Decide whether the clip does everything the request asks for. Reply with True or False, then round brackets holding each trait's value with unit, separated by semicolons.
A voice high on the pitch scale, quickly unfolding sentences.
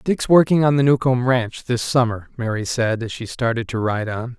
False (125 Hz; 220 wpm)